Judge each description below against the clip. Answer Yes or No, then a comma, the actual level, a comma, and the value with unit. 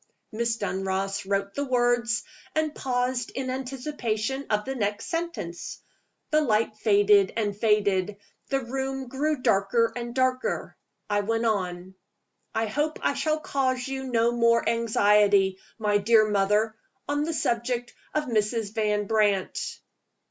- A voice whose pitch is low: No, high, 230 Hz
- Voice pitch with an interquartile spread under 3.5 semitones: No, average, 3.9 semitones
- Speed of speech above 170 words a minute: No, slow, 135 wpm